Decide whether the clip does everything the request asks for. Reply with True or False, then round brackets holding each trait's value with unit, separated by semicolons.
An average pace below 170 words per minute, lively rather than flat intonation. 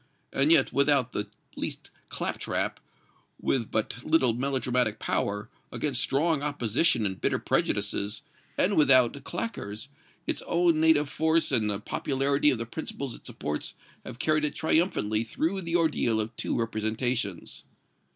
True (140 wpm; 5.7 semitones)